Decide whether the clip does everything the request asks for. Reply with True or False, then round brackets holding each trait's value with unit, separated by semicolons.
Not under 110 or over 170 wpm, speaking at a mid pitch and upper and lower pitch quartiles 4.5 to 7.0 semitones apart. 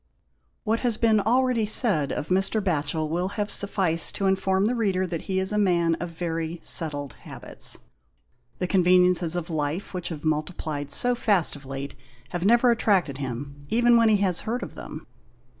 False (180 wpm; 180 Hz; 4.8 semitones)